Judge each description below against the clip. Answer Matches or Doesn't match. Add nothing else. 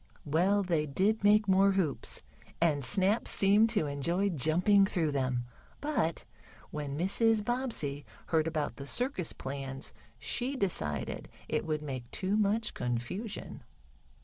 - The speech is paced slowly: Matches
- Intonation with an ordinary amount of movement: Doesn't match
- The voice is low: Doesn't match